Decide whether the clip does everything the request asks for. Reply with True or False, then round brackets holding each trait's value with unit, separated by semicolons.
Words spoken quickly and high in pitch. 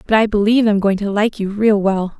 True (275 wpm; 205 Hz)